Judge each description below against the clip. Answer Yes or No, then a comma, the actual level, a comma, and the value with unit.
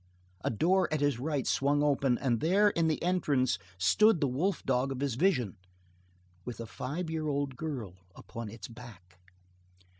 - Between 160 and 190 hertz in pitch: No, medium, 140 Hz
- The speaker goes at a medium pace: Yes, average, 170 wpm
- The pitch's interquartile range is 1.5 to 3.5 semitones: No, average, 5.0 semitones